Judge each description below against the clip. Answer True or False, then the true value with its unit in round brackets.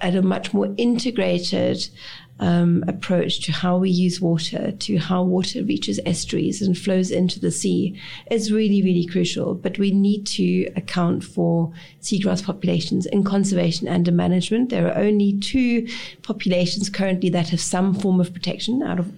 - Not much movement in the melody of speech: True (2.3 semitones)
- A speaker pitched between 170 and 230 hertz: True (185 Hz)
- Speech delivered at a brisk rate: False (165 wpm)